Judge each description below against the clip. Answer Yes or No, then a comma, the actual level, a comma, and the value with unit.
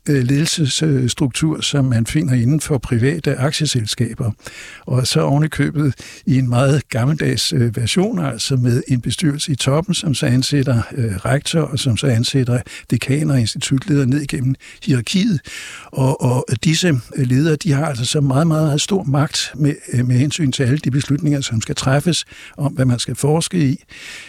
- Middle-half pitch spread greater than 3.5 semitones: No, average, 2.9 semitones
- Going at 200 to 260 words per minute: No, average, 160 wpm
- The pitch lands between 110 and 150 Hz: Yes, medium, 140 Hz